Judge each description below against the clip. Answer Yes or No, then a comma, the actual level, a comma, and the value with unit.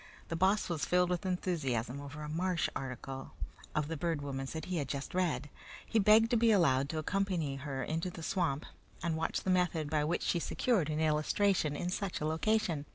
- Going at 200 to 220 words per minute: Yes, fast, 205 wpm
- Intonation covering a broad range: No, average, 4.1 semitones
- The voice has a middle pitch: Yes, medium, 160 Hz